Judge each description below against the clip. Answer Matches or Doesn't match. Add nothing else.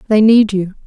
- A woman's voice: Matches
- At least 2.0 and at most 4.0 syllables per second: Doesn't match